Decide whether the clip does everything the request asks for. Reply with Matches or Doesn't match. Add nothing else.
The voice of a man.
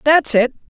Doesn't match